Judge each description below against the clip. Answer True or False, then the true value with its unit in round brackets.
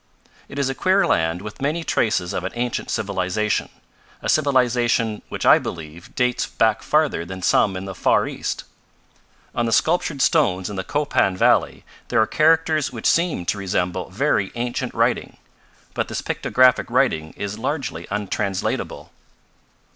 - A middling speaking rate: True (155 wpm)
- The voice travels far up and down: True (6.4 semitones)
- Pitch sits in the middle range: False (110 Hz)